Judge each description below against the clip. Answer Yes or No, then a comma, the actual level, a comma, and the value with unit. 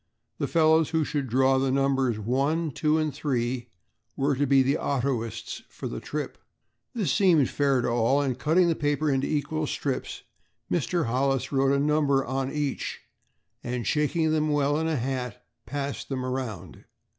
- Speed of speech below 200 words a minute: Yes, average, 170 wpm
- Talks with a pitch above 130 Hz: Yes, medium, 140 Hz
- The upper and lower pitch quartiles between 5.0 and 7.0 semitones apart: No, average, 2.7 semitones